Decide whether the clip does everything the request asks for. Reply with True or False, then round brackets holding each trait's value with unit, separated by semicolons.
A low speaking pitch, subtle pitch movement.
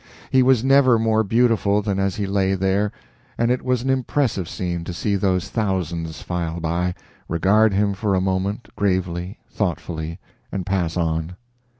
False (95 Hz; 3.8 semitones)